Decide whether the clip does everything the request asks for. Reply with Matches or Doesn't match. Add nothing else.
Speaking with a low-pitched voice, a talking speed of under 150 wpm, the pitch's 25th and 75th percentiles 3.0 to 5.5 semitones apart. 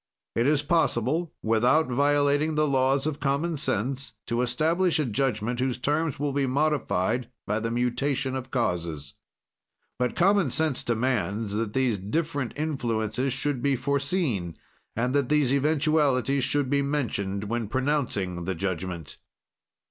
Matches